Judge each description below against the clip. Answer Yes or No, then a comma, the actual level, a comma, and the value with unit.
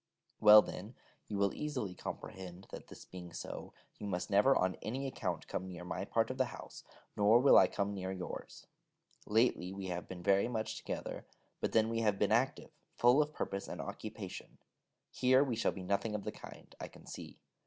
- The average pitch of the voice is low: Yes, low, 105 Hz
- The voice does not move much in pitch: No, average, 4.0 semitones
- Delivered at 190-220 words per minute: Yes, average, 195 wpm